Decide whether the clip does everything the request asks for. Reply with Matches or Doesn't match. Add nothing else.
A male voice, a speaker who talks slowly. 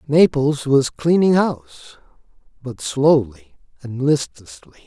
Matches